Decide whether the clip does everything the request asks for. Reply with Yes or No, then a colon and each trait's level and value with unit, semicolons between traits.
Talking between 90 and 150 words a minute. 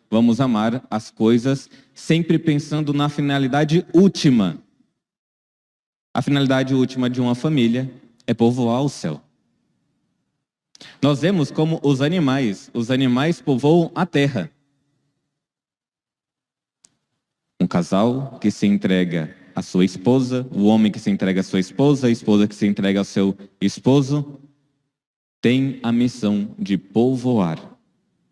Yes: average, 125 wpm